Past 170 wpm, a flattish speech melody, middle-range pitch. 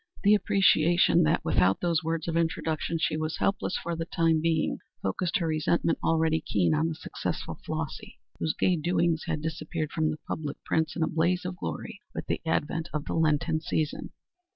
Yes: average, 185 wpm; narrow, 1.4 semitones; medium, 160 Hz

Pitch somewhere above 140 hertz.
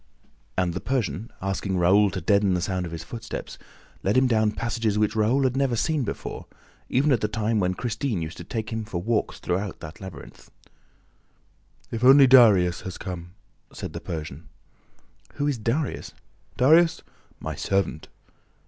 No: low, 105 Hz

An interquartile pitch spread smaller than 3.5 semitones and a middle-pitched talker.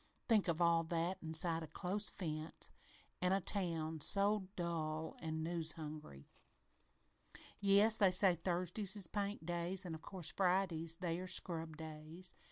Yes: average, 2.9 semitones; medium, 170 Hz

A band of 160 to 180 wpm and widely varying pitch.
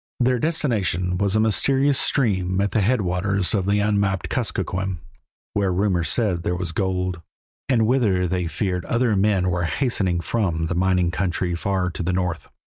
No: average, 165 wpm; average, 2.9 semitones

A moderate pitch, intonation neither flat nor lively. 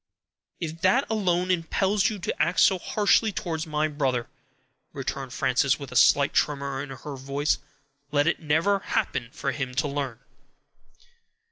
Yes: medium, 155 Hz; average, 4.8 semitones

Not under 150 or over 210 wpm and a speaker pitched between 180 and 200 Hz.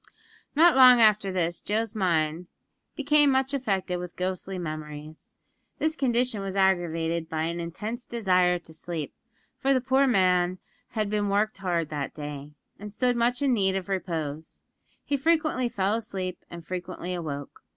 Yes: average, 155 wpm; high, 190 Hz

